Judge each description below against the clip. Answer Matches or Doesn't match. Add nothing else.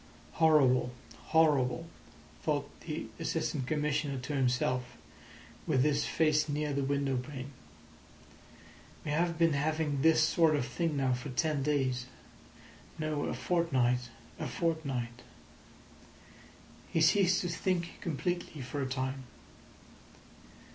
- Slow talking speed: Matches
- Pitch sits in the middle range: Matches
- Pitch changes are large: Doesn't match